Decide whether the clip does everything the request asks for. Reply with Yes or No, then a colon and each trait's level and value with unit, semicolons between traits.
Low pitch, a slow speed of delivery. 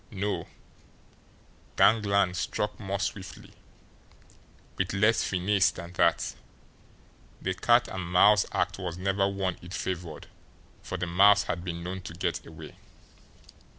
Yes: very low, 95 Hz; slow, 125 wpm